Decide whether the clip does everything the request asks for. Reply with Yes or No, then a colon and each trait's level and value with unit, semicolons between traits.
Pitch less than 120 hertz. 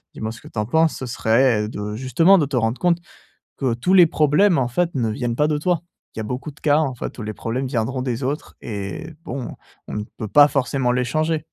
No: low, 130 Hz